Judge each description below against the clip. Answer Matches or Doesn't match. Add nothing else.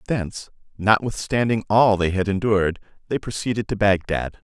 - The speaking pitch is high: Doesn't match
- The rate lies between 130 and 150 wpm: Matches